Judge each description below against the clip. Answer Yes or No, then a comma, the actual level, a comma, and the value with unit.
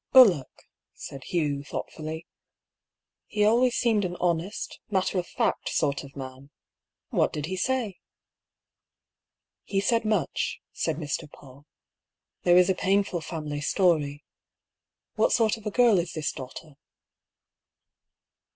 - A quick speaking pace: No, average, 145 wpm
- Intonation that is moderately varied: No, wide, 5.7 semitones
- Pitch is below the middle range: No, medium, 175 Hz